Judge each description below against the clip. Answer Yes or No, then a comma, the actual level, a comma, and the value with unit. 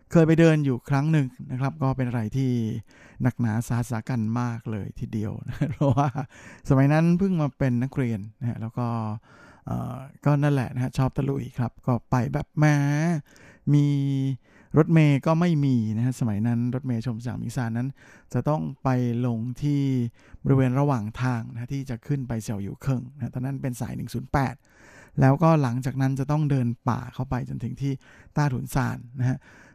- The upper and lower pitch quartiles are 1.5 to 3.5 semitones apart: Yes, average, 2.9 semitones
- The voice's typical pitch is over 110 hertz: Yes, low, 130 Hz